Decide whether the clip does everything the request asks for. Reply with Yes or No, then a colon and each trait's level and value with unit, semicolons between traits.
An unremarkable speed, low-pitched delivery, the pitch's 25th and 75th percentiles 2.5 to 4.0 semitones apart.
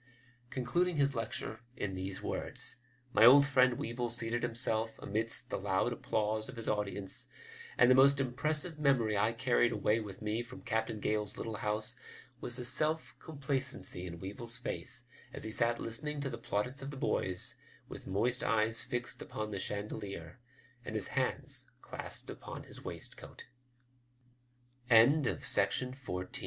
Yes: average, 150 wpm; low, 115 Hz; average, 3.3 semitones